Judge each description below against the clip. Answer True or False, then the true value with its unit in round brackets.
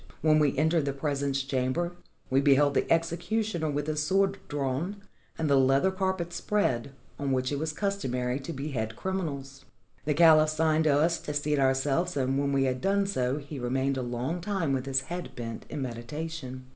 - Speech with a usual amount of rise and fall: True (3.8 semitones)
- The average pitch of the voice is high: False (145 Hz)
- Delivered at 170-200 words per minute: True (185 wpm)